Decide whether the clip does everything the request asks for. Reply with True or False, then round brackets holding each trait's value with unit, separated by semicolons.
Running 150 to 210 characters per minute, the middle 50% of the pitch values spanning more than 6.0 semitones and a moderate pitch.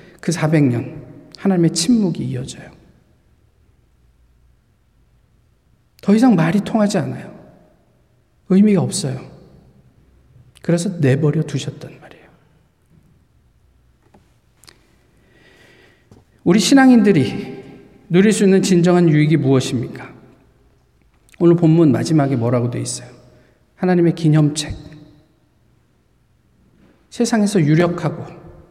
False (205 characters per minute; 5.1 semitones; 160 Hz)